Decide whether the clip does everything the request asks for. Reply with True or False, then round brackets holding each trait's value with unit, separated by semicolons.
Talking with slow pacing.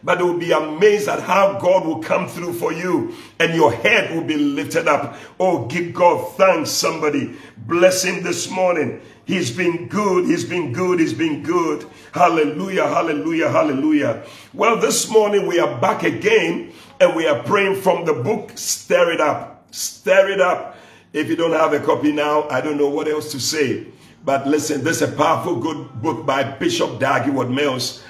False (185 wpm)